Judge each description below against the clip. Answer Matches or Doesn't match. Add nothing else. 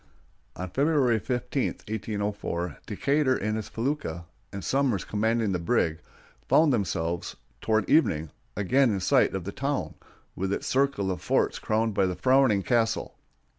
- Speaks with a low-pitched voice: Matches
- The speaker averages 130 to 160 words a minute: Matches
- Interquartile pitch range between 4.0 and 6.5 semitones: Matches